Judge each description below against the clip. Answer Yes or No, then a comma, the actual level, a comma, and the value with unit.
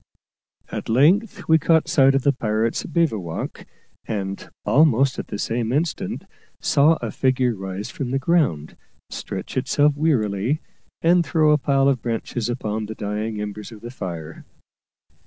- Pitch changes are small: No, wide, 5.6 semitones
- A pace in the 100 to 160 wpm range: Yes, average, 150 wpm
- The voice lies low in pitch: Yes, low, 125 Hz